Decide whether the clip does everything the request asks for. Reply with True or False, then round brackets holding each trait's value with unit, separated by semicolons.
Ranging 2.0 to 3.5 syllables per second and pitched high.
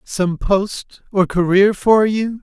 True (3.1 syllables/s; 200 Hz)